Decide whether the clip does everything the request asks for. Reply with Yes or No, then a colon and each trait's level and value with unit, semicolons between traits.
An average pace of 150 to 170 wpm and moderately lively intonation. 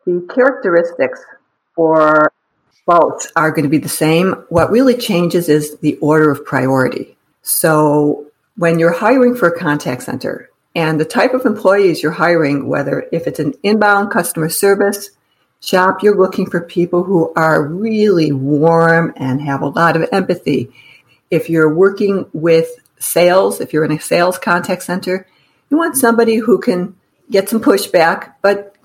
Yes: average, 160 wpm; average, 4.4 semitones